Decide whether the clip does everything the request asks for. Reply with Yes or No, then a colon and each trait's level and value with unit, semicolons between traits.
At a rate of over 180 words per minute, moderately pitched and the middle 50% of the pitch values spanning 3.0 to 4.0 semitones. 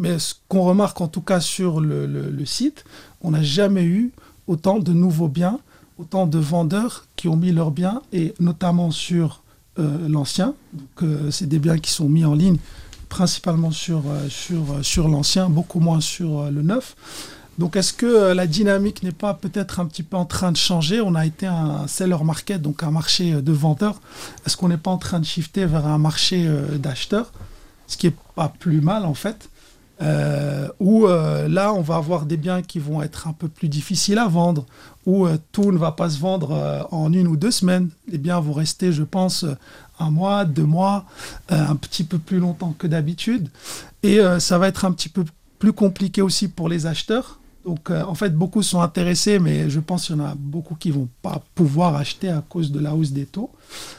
Yes: average, 215 wpm; medium, 170 Hz; average, 3.3 semitones